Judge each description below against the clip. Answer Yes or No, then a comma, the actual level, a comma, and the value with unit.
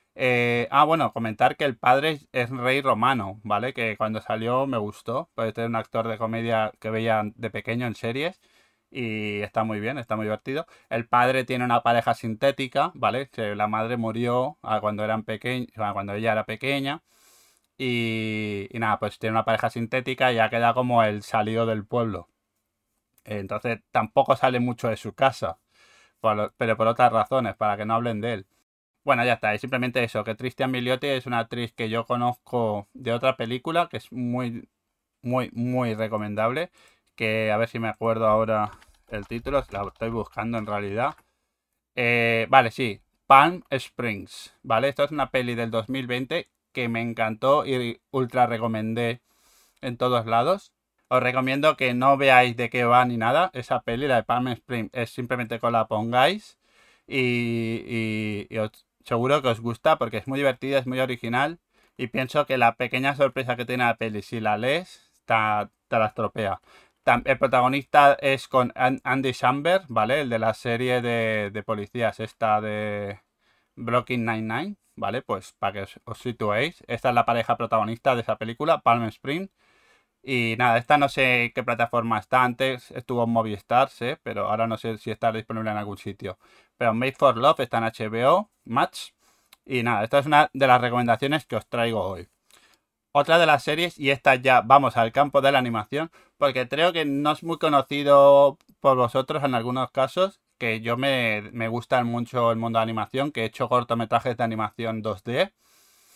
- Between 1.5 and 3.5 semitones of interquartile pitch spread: Yes, average, 2.8 semitones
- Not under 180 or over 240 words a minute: Yes, average, 185 wpm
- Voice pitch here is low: Yes, low, 120 Hz